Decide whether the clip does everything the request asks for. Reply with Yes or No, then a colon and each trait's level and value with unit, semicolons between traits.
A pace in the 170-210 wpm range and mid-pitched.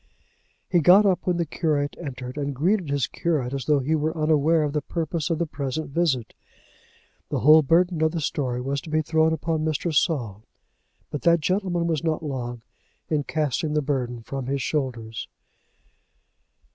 Yes: average, 175 wpm; medium, 150 Hz